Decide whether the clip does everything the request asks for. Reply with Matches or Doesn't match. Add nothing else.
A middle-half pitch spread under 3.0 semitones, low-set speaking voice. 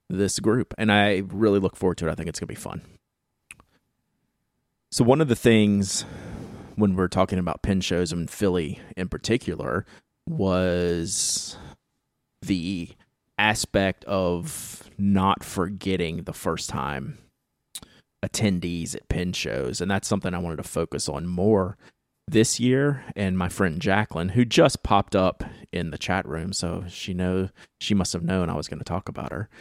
Matches